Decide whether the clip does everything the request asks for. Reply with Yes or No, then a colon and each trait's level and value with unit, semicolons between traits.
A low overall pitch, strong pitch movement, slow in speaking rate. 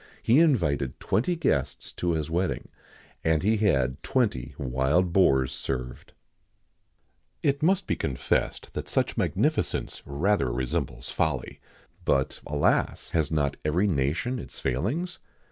Yes: very low, 80 Hz; wide, 7.7 semitones; slow, 130 wpm